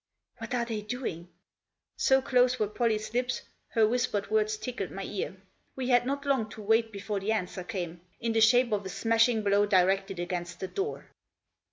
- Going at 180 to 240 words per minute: Yes, average, 200 wpm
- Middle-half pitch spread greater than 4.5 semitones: No, average, 3.8 semitones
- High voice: Yes, high, 215 Hz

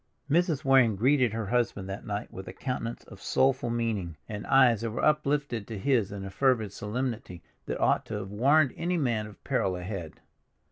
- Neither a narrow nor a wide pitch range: Yes, average, 4.7 semitones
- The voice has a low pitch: Yes, low, 115 Hz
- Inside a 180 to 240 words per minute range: Yes, average, 190 wpm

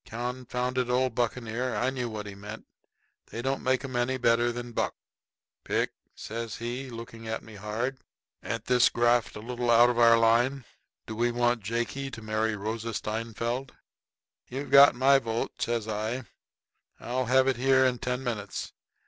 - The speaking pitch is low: Yes, low, 120 Hz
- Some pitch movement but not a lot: No, narrow, 2.0 semitones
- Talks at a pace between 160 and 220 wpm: Yes, average, 165 wpm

